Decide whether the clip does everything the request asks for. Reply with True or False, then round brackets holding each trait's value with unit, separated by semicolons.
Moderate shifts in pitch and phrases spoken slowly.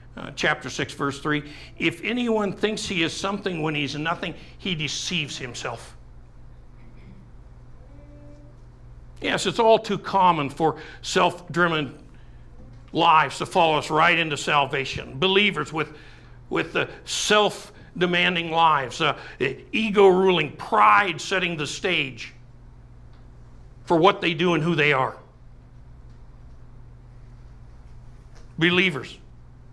False (6.7 semitones; 105 wpm)